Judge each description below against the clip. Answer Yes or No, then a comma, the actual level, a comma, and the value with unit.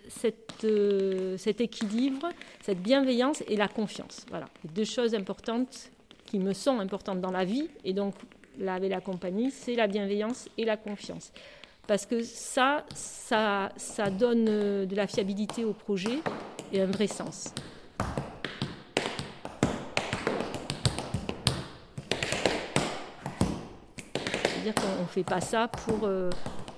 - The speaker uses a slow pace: Yes, slow, 130 wpm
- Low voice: No, high, 215 Hz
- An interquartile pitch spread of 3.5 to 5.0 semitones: No, average, 3.0 semitones